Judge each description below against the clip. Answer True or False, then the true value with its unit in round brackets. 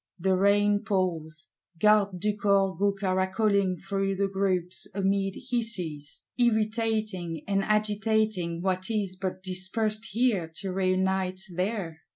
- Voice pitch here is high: True (195 Hz)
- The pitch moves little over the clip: True (2.2 semitones)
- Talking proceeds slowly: True (120 wpm)